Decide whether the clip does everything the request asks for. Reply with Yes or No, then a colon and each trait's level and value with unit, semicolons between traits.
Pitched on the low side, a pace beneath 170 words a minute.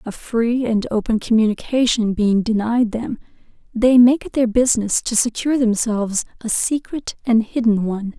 No: high, 230 Hz; average, 155 wpm